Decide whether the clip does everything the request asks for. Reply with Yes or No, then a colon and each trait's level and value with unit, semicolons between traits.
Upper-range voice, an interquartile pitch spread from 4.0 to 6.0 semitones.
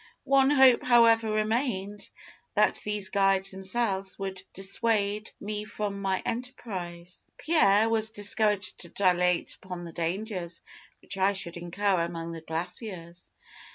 No: high, 195 Hz; average, 3.2 semitones